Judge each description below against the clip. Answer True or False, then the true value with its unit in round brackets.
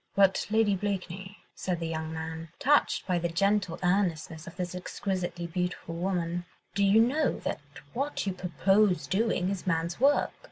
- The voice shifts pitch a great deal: False (2.9 semitones)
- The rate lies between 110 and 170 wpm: True (160 wpm)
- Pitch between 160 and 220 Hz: True (185 Hz)